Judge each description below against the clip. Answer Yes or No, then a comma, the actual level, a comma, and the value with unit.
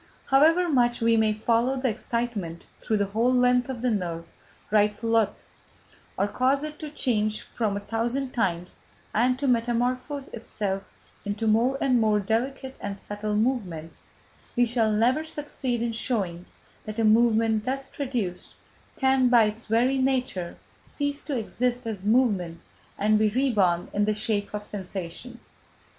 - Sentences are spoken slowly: No, average, 155 wpm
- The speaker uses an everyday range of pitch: Yes, average, 3.5 semitones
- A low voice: No, high, 230 Hz